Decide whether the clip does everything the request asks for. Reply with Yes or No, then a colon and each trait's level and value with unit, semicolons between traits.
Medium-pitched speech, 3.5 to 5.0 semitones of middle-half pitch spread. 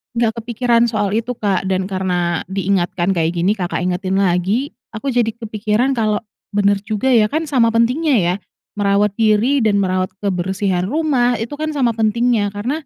No: high, 210 Hz; average, 3.9 semitones